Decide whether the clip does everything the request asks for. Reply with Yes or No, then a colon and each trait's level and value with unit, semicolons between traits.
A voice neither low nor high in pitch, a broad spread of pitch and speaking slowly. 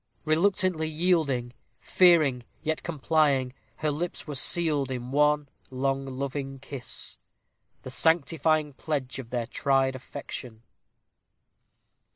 No: medium, 145 Hz; average, 3.2 semitones; slow, 105 wpm